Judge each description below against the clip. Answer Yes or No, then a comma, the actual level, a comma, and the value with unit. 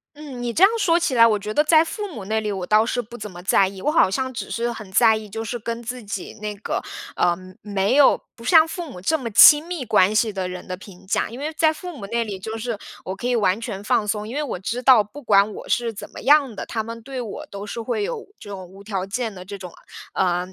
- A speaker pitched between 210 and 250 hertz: Yes, high, 225 Hz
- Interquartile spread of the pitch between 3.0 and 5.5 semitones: Yes, average, 4.5 semitones